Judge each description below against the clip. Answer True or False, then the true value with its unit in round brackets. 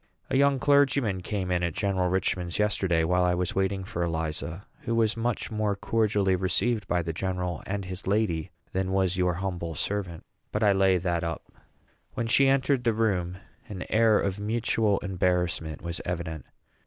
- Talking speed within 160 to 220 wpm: True (175 wpm)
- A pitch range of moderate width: True (3.4 semitones)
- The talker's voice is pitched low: True (95 Hz)